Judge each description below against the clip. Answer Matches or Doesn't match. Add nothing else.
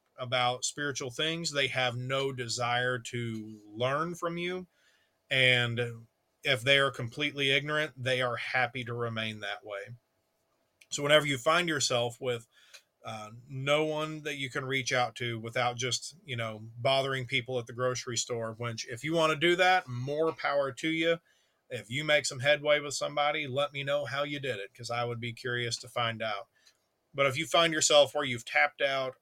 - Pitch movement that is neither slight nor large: Matches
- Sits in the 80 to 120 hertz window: Doesn't match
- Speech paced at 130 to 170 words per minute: Doesn't match